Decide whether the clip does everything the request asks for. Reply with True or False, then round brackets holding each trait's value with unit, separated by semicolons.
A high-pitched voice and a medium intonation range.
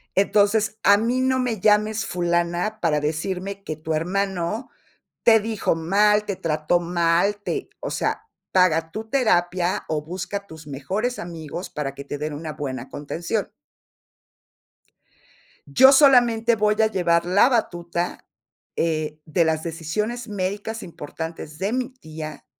False (180 Hz; 5.0 semitones)